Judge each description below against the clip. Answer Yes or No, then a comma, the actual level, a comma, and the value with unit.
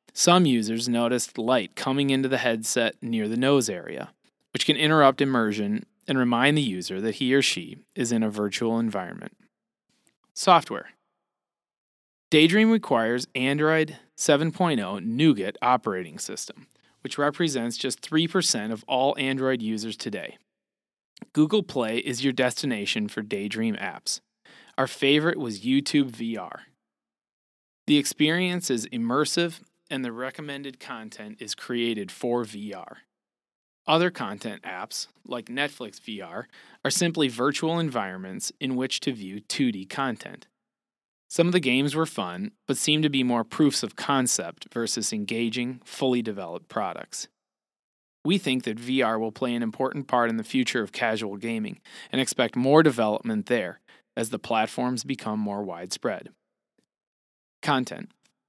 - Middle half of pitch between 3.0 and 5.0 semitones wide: No, wide, 5.4 semitones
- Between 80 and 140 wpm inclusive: Yes, slow, 135 wpm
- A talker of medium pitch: No, low, 130 Hz